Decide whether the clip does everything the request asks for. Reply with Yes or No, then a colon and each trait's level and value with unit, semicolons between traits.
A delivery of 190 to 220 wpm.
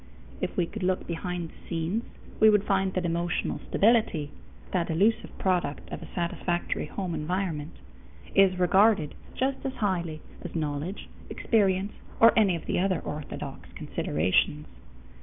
No: average, 140 wpm